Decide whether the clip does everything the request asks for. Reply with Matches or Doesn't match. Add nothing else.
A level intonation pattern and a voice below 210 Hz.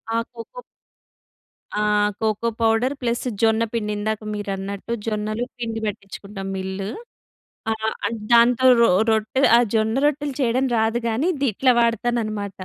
Doesn't match